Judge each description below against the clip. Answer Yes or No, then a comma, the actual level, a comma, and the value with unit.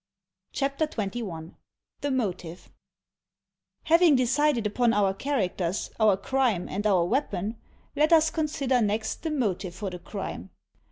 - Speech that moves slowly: Yes, slow, 125 wpm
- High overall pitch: Yes, high, 220 Hz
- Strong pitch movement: Yes, wide, 6.4 semitones